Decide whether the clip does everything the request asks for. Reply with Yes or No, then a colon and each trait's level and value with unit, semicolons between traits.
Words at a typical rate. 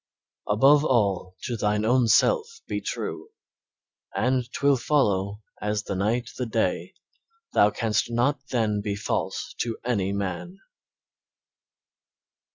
No: slow, 120 wpm